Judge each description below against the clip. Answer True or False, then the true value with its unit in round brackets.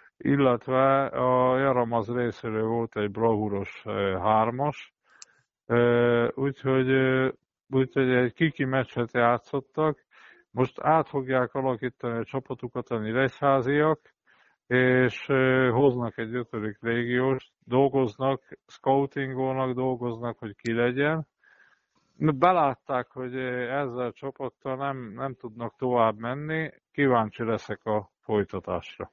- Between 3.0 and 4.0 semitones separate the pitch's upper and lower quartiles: False (2.4 semitones)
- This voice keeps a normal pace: False (95 wpm)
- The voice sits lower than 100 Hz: False (125 Hz)